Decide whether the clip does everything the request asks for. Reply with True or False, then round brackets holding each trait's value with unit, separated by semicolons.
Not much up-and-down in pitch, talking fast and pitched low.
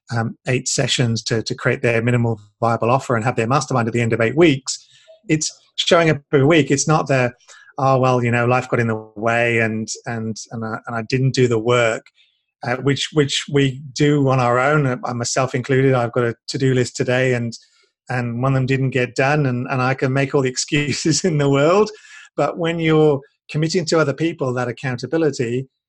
False (3.0 semitones; 215 wpm; 130 Hz)